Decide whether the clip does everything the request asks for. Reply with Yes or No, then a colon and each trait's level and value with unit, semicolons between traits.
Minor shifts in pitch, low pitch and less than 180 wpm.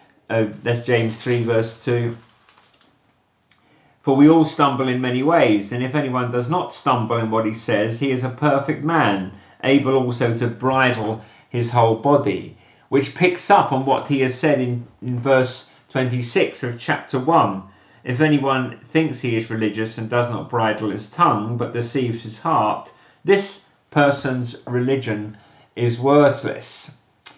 No: average, 3.5 semitones; low, 125 Hz; average, 155 wpm